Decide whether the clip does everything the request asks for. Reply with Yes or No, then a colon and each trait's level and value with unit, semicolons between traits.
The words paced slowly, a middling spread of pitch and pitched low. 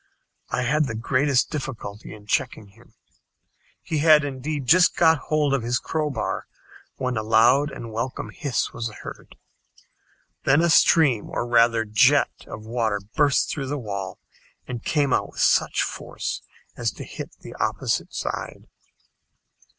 No: average, 150 wpm; average, 4.5 semitones; low, 125 Hz